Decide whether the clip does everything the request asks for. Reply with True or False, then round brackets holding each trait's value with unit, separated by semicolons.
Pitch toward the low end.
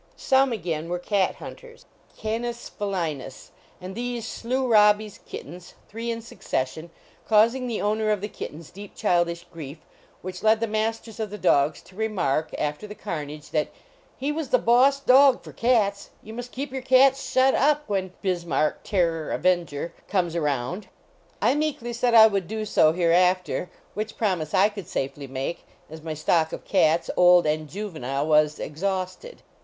False (200 Hz)